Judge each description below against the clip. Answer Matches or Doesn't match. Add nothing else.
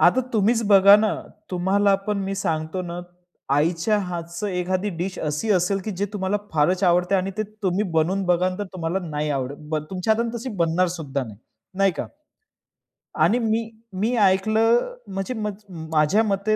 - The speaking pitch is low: Doesn't match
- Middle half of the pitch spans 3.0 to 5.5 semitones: Matches